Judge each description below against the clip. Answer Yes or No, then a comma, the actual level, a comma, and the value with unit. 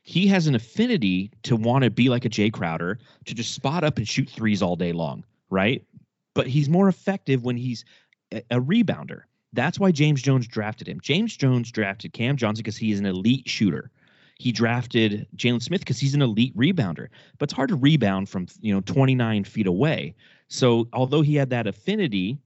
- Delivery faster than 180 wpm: Yes, average, 200 wpm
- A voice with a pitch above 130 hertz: No, low, 125 Hz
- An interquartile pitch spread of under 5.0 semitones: No, wide, 5.4 semitones